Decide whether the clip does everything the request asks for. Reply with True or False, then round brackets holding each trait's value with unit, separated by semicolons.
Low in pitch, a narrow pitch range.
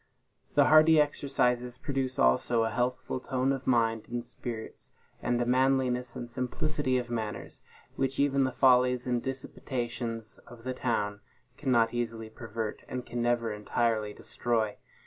True (125 Hz; 2.1 semitones)